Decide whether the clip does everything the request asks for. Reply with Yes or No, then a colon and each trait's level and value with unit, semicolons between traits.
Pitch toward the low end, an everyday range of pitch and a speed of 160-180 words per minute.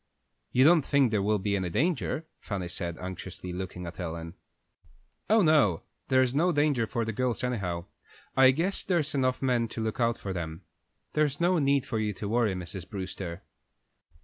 No: low, 115 Hz; wide, 6.9 semitones; average, 175 wpm